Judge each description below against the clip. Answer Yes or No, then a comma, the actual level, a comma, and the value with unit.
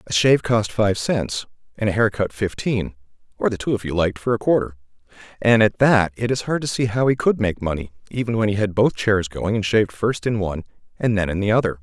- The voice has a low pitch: Yes, low, 105 Hz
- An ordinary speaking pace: No, fast, 250 wpm